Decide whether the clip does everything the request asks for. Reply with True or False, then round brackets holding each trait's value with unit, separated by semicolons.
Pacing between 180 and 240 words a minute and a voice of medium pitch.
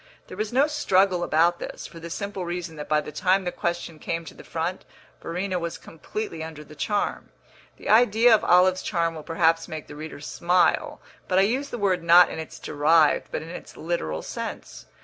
True (205 wpm; 170 Hz)